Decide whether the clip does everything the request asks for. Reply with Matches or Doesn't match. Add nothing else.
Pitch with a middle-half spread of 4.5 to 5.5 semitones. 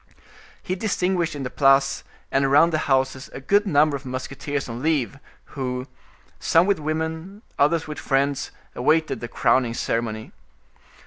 Doesn't match